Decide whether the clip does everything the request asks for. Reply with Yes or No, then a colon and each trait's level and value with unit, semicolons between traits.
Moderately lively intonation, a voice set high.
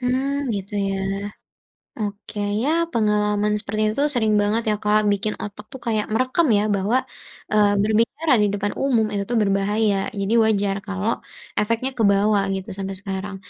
No: narrow, 2.0 semitones; high, 210 Hz